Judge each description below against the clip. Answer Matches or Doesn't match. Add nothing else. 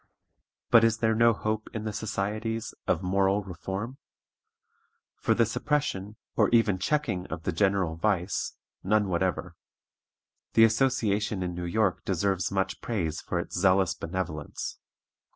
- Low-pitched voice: Matches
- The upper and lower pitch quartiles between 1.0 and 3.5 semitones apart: Matches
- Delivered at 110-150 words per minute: Matches